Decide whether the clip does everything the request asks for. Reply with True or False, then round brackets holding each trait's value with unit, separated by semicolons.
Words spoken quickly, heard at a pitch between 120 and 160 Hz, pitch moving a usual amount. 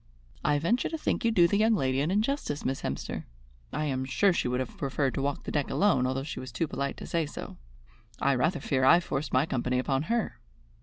True (235 wpm; 140 Hz; 4.8 semitones)